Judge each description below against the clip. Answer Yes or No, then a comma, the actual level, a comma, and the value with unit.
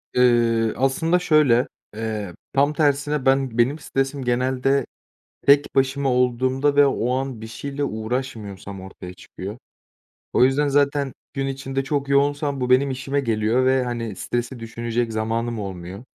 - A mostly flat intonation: No, average, 3.2 semitones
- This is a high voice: No, low, 130 Hz